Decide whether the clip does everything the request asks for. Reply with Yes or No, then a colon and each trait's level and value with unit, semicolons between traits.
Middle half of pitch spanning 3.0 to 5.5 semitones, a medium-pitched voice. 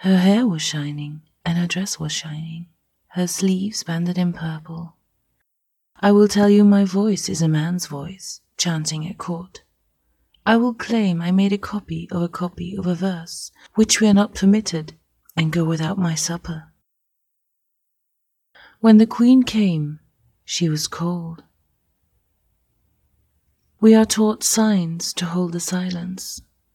Yes: average, 3.7 semitones; medium, 175 Hz